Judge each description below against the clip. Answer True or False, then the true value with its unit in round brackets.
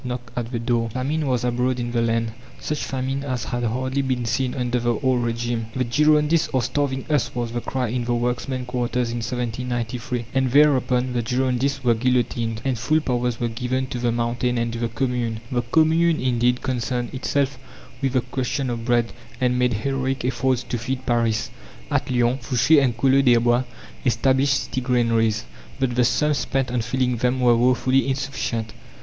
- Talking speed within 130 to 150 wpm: False (185 wpm)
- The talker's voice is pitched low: True (125 Hz)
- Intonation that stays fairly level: True (1.8 semitones)